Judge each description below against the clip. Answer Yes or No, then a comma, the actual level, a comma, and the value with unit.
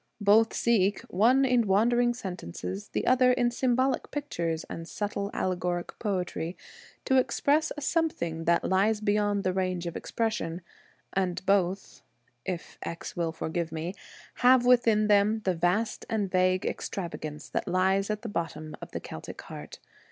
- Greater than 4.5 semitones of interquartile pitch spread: Yes, average, 4.9 semitones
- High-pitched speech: Yes, high, 195 Hz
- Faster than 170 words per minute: No, average, 155 wpm